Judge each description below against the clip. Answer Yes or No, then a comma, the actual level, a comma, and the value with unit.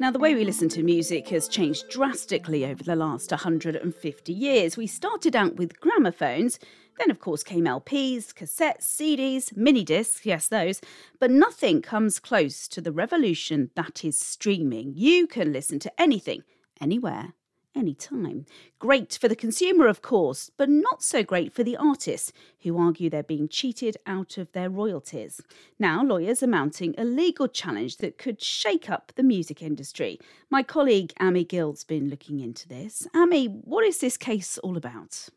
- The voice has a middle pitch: No, high, 215 Hz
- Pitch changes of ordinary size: No, wide, 8.8 semitones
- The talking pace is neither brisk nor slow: Yes, average, 170 wpm